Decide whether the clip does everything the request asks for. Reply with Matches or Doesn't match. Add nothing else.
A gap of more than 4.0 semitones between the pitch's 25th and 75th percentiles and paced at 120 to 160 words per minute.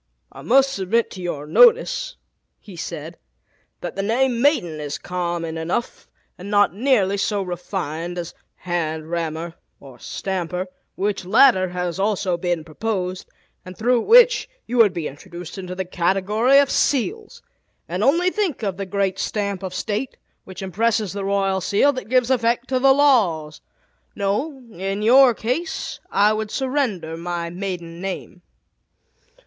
Matches